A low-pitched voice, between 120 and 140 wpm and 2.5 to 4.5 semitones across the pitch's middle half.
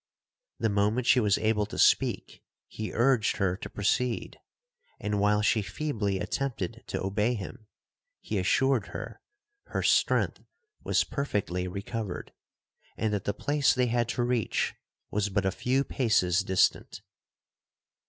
Yes: low, 110 Hz; slow, 135 wpm; average, 3.7 semitones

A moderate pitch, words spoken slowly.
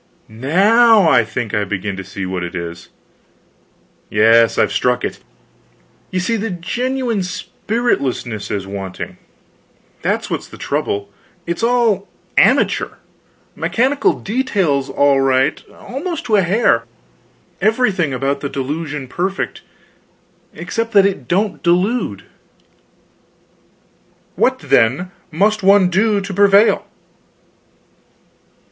Yes: medium, 175 Hz; slow, 110 wpm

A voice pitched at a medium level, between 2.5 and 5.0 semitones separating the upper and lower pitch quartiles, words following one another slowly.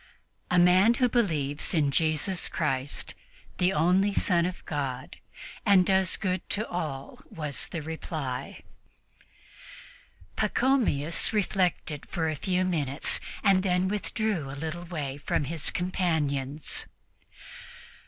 Yes: medium, 170 Hz; average, 4.3 semitones; slow, 115 wpm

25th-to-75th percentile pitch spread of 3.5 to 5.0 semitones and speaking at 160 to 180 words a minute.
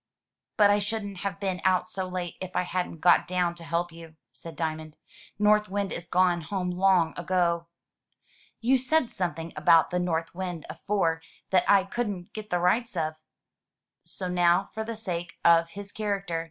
No: average, 2.9 semitones; average, 175 wpm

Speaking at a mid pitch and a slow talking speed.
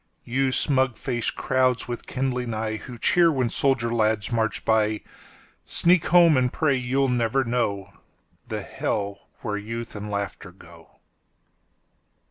No: low, 120 Hz; slow, 120 wpm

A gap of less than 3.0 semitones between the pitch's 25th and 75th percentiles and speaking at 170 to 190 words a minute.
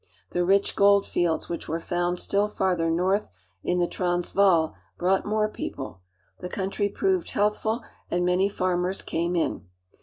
No: narrow, 2.4 semitones; average, 160 wpm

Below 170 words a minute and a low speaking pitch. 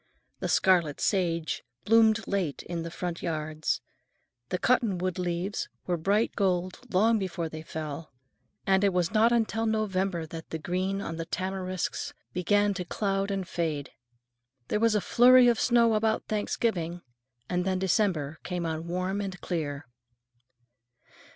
No: average, 145 wpm; medium, 185 Hz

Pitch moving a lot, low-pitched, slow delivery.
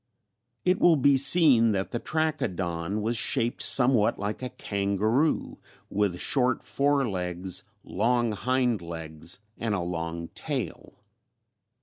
Yes: wide, 6.1 semitones; low, 110 Hz; slow, 120 wpm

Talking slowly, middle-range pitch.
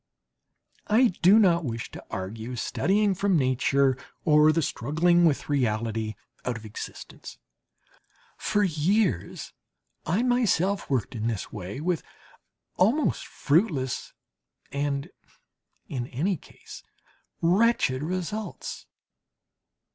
Yes: slow, 100 wpm; medium, 150 Hz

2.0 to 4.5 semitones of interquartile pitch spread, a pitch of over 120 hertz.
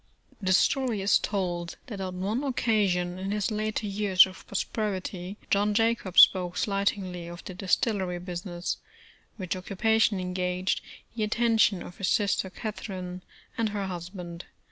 Yes: average, 2.7 semitones; high, 190 Hz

